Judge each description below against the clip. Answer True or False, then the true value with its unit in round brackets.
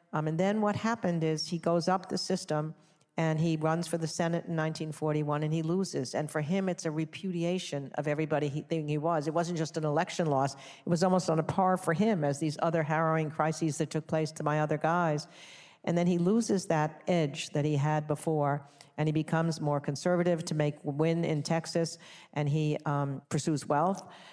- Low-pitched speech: False (160 Hz)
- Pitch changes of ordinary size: False (2.2 semitones)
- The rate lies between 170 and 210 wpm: True (205 wpm)